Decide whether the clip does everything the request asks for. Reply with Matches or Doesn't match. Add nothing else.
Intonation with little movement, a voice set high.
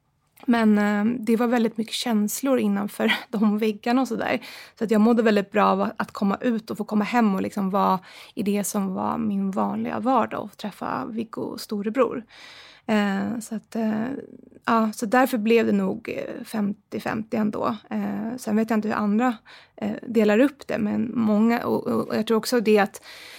Matches